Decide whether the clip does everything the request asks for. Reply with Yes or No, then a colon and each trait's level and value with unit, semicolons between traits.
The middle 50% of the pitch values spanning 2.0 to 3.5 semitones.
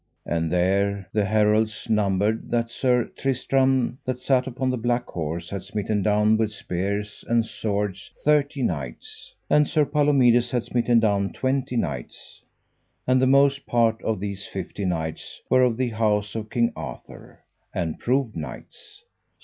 No: average, 4.2 semitones